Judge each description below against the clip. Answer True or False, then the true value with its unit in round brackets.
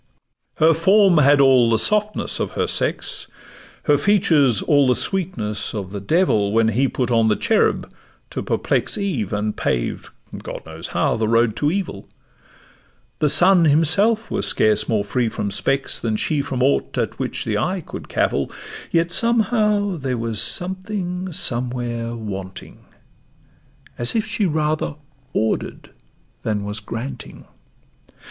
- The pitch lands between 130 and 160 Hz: True (135 Hz)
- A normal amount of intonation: False (8.6 semitones)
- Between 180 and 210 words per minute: False (145 wpm)